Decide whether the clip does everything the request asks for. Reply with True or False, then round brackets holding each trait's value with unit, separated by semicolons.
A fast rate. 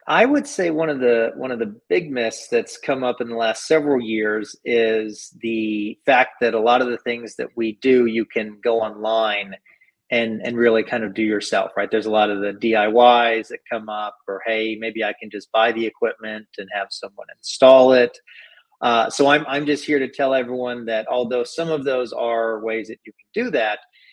True (215 wpm)